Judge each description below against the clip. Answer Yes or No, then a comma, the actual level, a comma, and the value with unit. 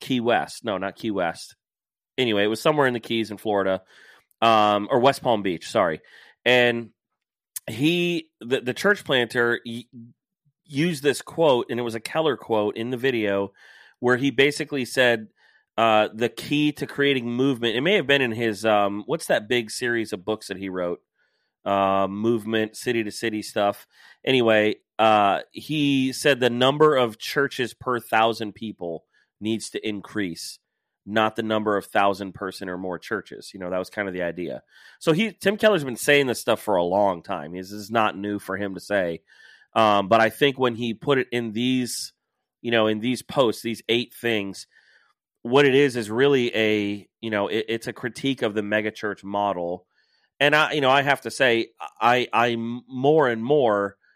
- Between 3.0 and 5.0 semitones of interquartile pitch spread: Yes, average, 3.9 semitones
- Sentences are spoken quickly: No, average, 185 wpm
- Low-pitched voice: Yes, low, 115 Hz